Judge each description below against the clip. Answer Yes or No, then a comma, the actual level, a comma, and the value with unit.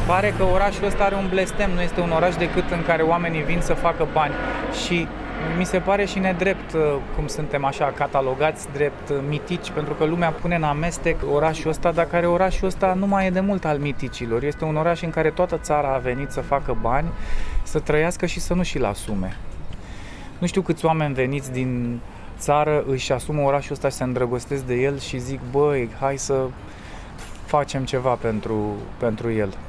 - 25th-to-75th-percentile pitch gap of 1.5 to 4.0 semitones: No, average, 4.8 semitones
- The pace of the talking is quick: Yes, fast, 190 wpm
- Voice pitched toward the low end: No, medium, 150 Hz